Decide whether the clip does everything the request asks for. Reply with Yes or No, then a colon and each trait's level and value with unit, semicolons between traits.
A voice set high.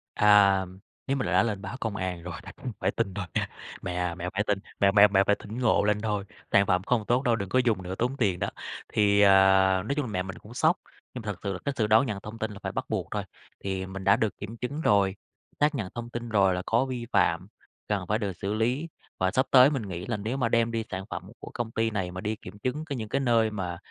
No: low, 105 Hz